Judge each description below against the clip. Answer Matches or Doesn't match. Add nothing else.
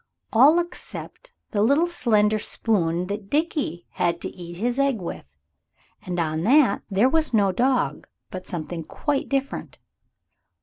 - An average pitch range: Doesn't match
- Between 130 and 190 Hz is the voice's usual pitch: Doesn't match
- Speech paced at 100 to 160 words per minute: Matches